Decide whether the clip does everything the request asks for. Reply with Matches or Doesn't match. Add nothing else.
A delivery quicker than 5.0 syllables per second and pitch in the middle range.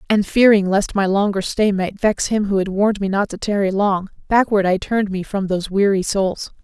Doesn't match